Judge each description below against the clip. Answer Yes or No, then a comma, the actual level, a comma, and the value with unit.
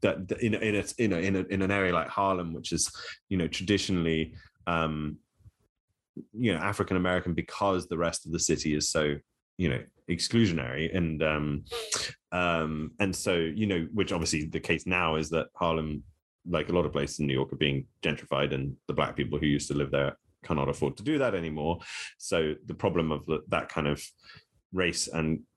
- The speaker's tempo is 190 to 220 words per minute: Yes, average, 195 wpm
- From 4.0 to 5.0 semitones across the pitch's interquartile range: No, average, 3.4 semitones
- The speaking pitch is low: Yes, very low, 80 Hz